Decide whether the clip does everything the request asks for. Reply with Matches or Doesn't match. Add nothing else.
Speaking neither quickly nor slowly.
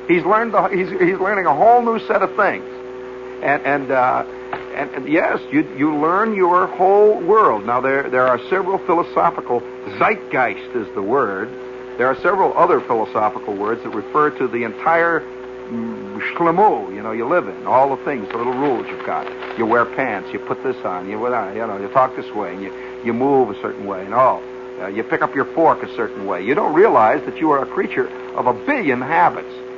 Doesn't match